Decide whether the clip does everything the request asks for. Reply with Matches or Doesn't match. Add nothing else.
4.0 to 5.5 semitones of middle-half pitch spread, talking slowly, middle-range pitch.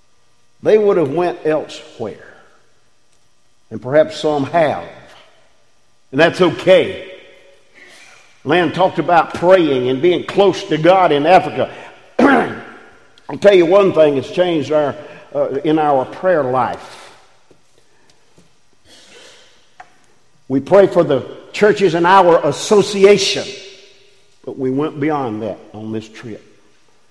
Matches